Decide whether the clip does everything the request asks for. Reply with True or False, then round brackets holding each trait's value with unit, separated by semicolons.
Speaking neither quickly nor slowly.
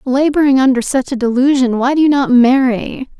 True (190 wpm)